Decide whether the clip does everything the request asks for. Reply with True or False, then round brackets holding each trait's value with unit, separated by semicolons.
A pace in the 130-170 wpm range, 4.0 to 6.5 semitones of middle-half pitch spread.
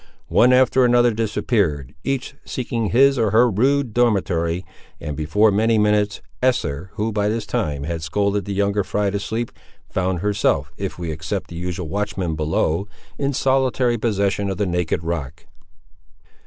True (155 wpm; 5.1 semitones)